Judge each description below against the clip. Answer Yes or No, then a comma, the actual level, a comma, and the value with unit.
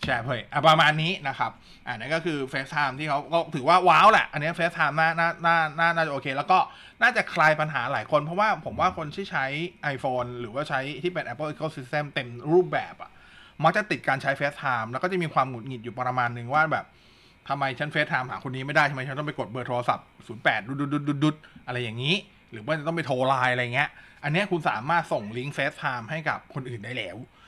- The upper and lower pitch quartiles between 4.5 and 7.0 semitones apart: No, average, 3.7 semitones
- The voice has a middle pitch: Yes, medium, 145 Hz